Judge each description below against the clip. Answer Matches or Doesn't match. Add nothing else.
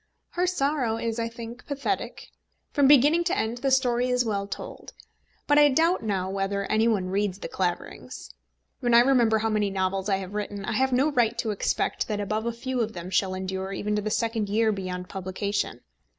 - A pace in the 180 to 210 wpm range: Matches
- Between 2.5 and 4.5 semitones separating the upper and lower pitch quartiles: Matches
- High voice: Matches